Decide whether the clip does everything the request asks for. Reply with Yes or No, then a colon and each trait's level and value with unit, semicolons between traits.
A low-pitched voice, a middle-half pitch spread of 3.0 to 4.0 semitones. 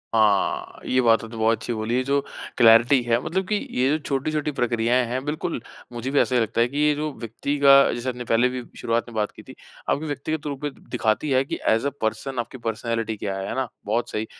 Yes: low, 125 Hz; average, 3.4 semitones